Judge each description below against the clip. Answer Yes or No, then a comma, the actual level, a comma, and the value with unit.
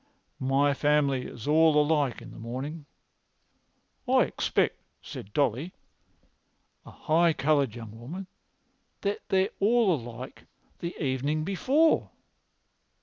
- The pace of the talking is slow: Yes, slow, 115 wpm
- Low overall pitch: No, medium, 150 Hz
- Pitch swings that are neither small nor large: Yes, average, 4.8 semitones